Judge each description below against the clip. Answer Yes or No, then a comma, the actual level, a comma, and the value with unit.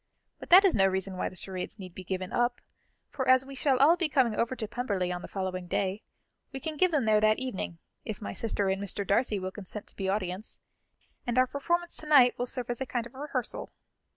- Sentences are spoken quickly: Yes, fast, 235 wpm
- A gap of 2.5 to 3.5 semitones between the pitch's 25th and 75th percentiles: No, wide, 5.4 semitones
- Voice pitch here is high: Yes, high, 225 Hz